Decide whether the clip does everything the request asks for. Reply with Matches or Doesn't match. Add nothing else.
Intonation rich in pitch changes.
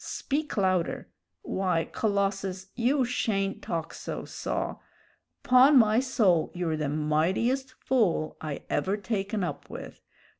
Matches